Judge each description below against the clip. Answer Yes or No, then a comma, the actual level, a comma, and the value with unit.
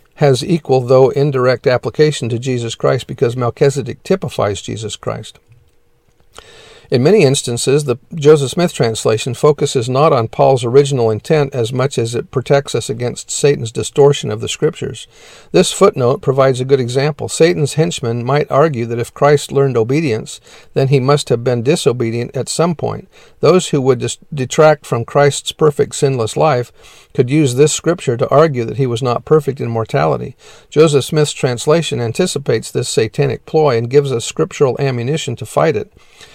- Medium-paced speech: Yes, average, 165 wpm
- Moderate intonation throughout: Yes, average, 3.8 semitones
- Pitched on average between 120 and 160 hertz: Yes, medium, 140 Hz